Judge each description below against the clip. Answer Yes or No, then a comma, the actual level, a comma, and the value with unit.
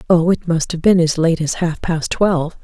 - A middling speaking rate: No, fast, 250 wpm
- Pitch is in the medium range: Yes, medium, 165 Hz